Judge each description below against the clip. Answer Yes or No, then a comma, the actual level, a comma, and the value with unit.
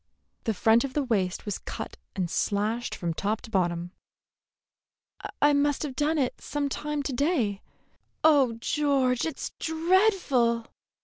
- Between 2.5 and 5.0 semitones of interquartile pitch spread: No, wide, 5.4 semitones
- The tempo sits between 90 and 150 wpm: Yes, average, 140 wpm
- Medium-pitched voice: No, very high, 255 Hz